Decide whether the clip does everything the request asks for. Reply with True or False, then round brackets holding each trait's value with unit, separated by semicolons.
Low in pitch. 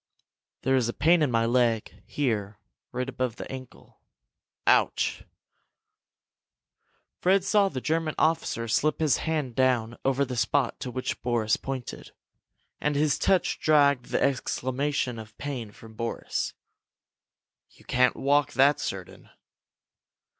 True (130 Hz)